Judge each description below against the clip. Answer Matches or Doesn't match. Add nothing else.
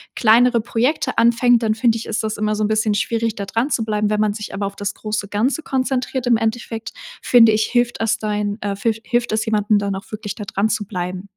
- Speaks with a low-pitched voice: Doesn't match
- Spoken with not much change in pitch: Matches